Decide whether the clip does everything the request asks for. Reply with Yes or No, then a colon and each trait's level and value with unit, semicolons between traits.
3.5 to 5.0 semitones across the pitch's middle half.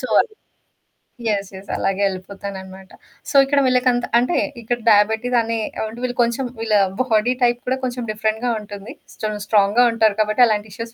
No: average, 2.9 semitones